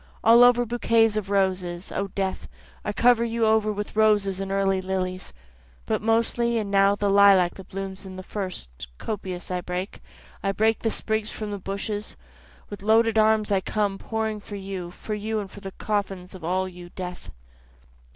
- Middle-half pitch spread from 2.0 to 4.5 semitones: Yes, narrow, 2.5 semitones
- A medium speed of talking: Yes, average, 180 wpm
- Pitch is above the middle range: Yes, high, 200 Hz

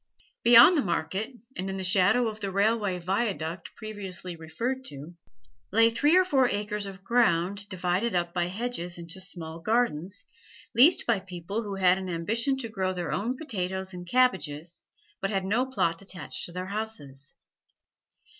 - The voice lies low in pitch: No, high, 195 Hz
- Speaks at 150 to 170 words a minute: Yes, average, 165 wpm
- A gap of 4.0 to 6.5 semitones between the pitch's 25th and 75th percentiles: Yes, average, 4.3 semitones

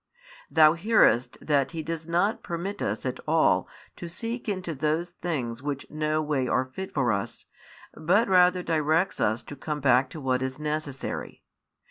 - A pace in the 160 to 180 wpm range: Yes, average, 165 wpm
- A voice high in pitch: No, medium, 155 Hz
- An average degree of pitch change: Yes, average, 4.3 semitones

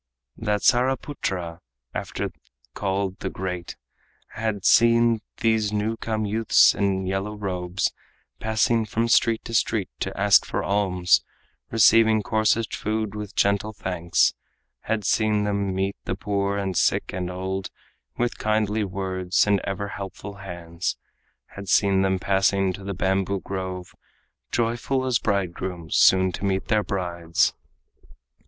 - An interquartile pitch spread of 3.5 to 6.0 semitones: No, narrow, 2.5 semitones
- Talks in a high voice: No, low, 100 Hz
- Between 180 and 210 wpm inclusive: No, slow, 135 wpm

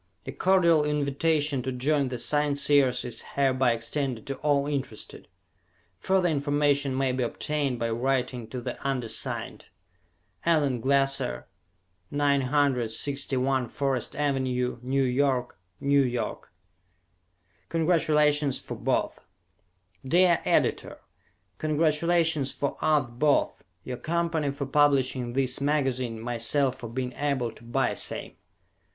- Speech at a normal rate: No, slow, 110 wpm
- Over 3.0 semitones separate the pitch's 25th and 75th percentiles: No, average, 2.7 semitones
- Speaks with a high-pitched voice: No, medium, 140 Hz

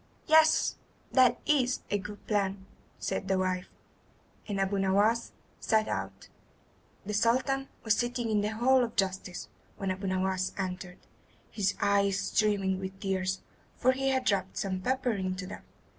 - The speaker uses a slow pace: No, average, 150 wpm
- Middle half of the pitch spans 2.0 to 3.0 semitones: No, average, 3.8 semitones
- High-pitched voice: Yes, high, 200 Hz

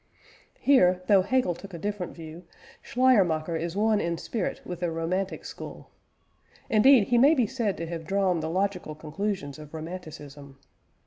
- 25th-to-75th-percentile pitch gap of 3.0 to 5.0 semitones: Yes, average, 4.2 semitones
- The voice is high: No, medium, 180 Hz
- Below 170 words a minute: Yes, average, 155 wpm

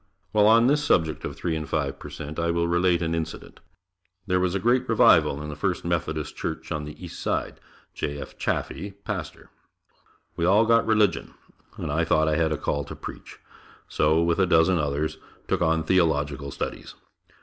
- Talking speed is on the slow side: No, average, 190 wpm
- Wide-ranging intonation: No, average, 3.2 semitones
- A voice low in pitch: Yes, very low, 80 Hz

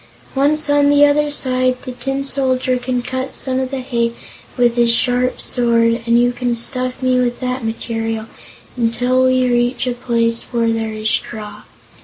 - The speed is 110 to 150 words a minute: No, average, 175 wpm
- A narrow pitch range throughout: Yes, narrow, 1.7 semitones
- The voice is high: Yes, very high, 250 Hz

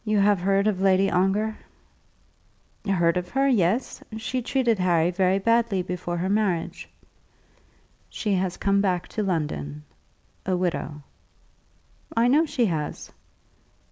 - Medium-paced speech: No, slow, 130 wpm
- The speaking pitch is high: Yes, high, 195 Hz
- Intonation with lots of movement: No, average, 3.3 semitones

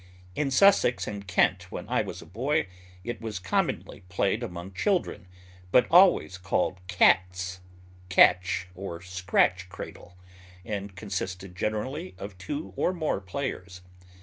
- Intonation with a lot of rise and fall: No, average, 4.8 semitones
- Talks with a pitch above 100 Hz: No, very low, 95 Hz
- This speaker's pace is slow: Yes, slow, 130 wpm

